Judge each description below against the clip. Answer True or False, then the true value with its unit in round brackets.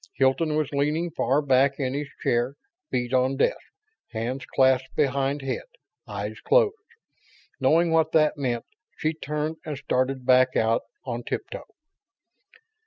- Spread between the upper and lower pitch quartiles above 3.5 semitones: False (2.9 semitones)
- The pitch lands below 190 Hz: True (135 Hz)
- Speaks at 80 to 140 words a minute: True (135 wpm)